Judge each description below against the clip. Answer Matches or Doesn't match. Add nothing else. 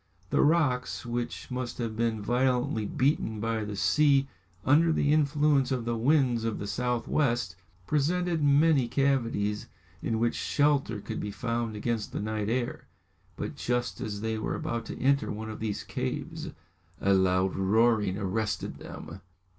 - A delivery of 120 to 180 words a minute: Matches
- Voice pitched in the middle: Doesn't match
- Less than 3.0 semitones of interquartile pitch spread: Doesn't match